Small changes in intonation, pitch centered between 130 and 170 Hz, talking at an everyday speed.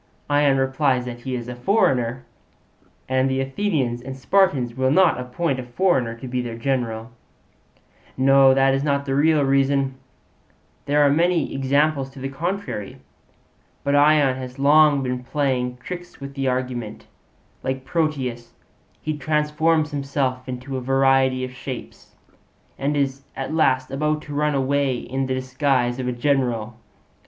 Yes: narrow, 2.3 semitones; low, 135 Hz; average, 150 wpm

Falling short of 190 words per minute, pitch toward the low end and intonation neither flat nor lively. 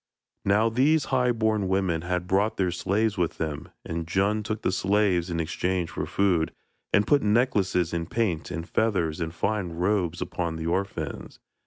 Yes: average, 170 wpm; very low, 95 Hz; average, 3.9 semitones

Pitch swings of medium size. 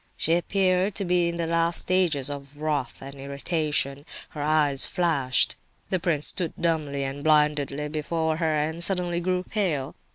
Yes: average, 3.2 semitones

